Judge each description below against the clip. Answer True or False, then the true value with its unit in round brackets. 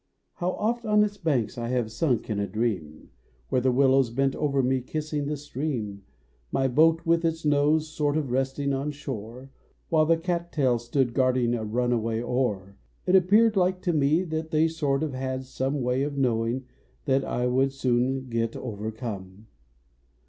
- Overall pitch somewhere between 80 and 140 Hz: True (135 Hz)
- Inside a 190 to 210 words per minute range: False (175 wpm)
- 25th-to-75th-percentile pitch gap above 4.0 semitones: True (4.4 semitones)